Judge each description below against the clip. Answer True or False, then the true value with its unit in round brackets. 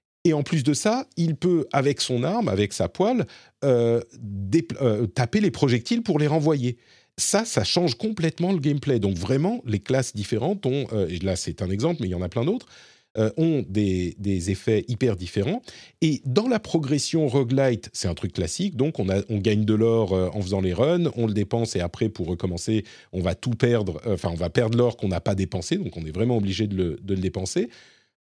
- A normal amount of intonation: False (7.0 semitones)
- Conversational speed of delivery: False (225 wpm)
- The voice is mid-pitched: False (115 Hz)